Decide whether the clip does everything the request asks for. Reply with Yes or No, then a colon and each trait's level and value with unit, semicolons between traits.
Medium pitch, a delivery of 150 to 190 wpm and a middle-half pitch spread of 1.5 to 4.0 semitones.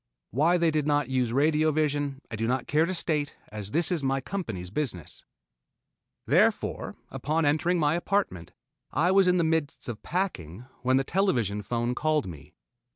No: medium, 145 Hz; average, 170 wpm; average, 5.3 semitones